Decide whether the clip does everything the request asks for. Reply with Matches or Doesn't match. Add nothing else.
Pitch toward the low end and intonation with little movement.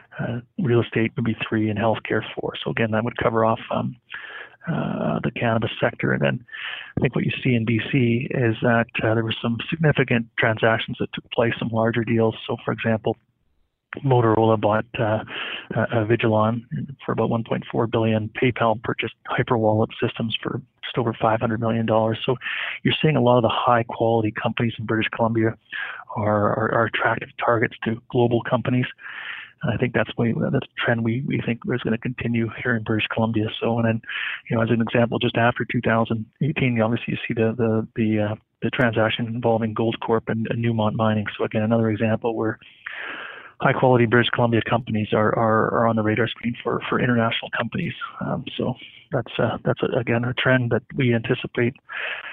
Matches